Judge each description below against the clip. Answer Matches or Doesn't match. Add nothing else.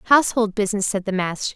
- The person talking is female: Matches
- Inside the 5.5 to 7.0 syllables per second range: Matches